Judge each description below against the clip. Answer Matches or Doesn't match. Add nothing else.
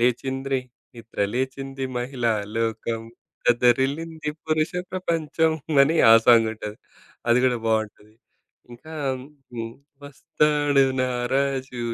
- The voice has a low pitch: Matches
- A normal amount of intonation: Matches